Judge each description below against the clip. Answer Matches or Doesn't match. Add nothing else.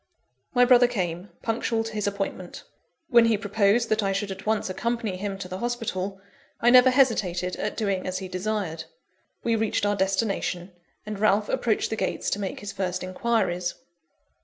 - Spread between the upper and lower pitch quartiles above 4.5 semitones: Doesn't match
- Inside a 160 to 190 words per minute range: Matches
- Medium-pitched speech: Doesn't match